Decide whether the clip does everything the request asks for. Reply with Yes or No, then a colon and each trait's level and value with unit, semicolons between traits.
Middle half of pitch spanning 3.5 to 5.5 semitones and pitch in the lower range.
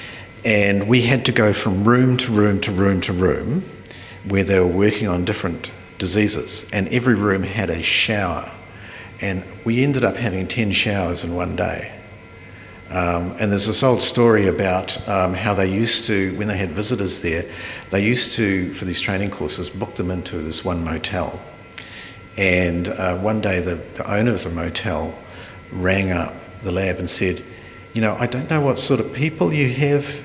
Yes: average, 3.8 semitones; low, 100 Hz